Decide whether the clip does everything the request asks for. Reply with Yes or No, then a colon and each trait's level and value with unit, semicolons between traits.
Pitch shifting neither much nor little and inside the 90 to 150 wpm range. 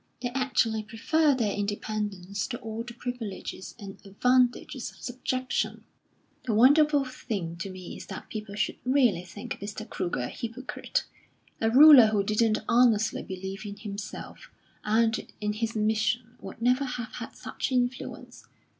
Yes: average, 3.4 semitones; average, 145 wpm